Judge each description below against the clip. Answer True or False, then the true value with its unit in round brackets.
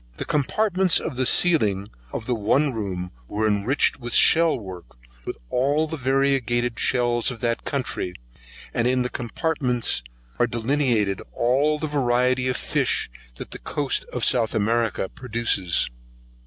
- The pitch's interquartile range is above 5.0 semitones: False (3.8 semitones)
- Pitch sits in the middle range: False (125 Hz)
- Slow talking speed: False (145 wpm)